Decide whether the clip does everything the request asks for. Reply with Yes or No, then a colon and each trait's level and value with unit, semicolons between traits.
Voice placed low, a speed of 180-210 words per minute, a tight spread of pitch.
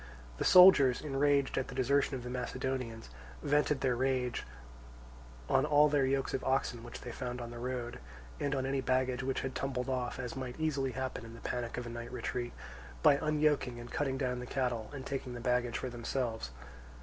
Yes: low, 130 Hz; average, 195 wpm; narrow, 1.8 semitones